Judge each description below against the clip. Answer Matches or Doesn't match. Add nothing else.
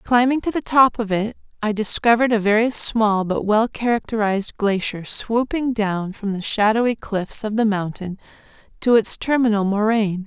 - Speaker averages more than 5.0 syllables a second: Doesn't match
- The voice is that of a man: Doesn't match